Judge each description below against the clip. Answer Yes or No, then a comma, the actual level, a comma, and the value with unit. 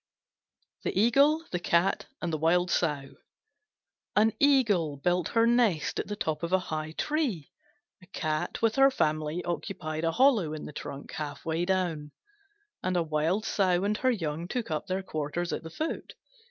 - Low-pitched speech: No, medium, 175 Hz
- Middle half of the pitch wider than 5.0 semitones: Yes, wide, 5.4 semitones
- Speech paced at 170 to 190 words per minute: Yes, average, 175 wpm